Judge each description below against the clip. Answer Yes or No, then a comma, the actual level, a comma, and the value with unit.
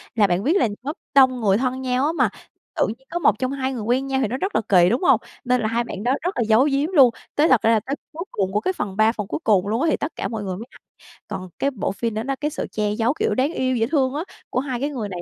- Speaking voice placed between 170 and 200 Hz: No, very high, 250 Hz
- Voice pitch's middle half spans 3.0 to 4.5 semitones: Yes, average, 4.2 semitones